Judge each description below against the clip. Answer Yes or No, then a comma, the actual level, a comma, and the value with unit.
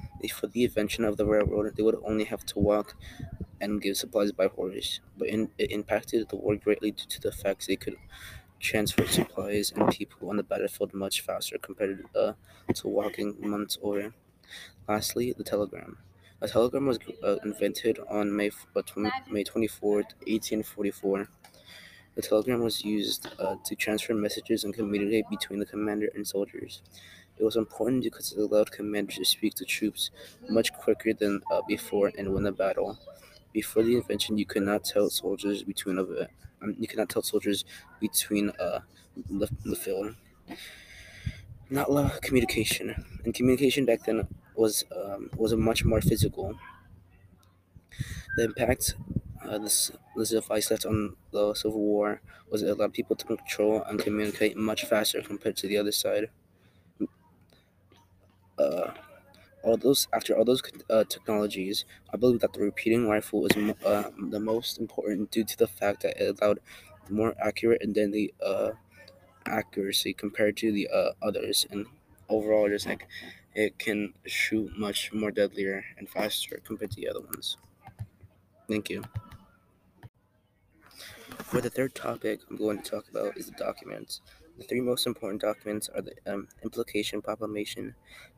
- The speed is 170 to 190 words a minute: No, average, 160 wpm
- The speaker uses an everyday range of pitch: No, narrow, 1.7 semitones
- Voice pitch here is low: Yes, low, 105 Hz